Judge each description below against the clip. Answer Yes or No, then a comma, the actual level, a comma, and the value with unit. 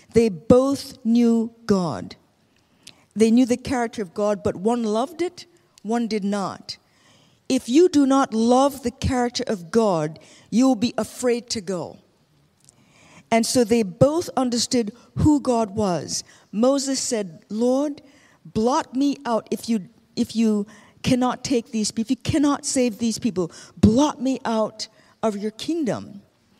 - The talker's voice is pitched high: Yes, high, 230 Hz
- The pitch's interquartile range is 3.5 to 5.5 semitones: No, average, 3.0 semitones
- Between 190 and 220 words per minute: No, average, 150 wpm